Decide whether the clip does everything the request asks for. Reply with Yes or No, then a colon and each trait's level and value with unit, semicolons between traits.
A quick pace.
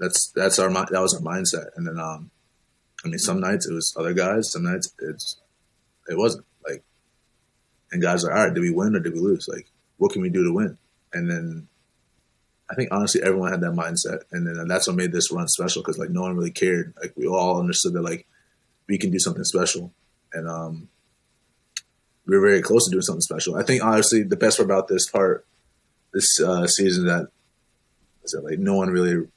Yes: fast, 220 wpm